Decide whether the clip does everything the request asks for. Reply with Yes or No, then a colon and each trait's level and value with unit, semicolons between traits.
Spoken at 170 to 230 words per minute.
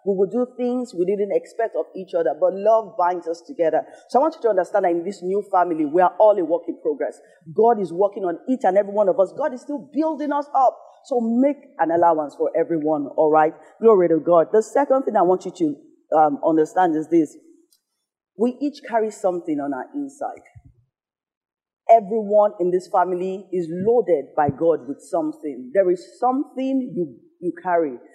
Yes: average, 200 wpm